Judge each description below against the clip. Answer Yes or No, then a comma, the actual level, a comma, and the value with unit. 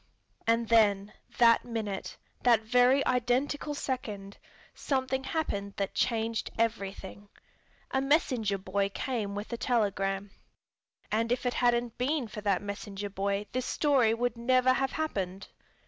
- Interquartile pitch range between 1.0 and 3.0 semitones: No, average, 3.9 semitones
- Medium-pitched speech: No, high, 230 Hz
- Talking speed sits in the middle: No, slow, 130 wpm